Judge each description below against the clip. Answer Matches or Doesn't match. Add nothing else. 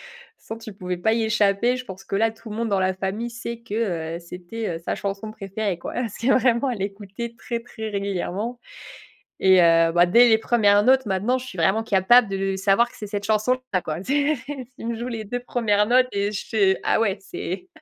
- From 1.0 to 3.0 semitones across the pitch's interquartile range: Doesn't match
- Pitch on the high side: Matches